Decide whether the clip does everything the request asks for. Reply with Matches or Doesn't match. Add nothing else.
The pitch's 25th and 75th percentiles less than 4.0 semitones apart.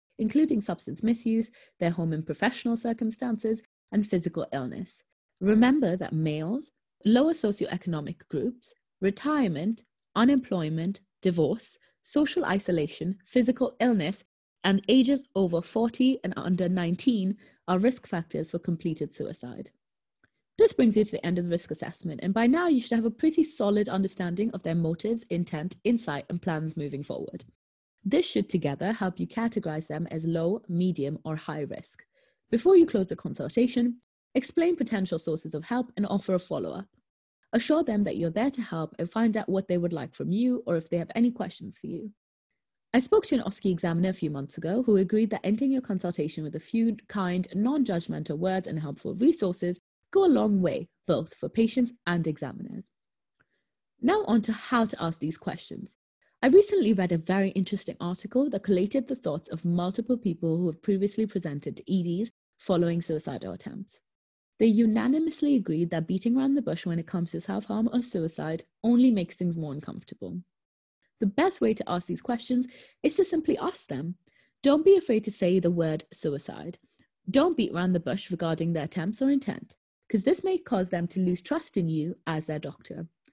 Doesn't match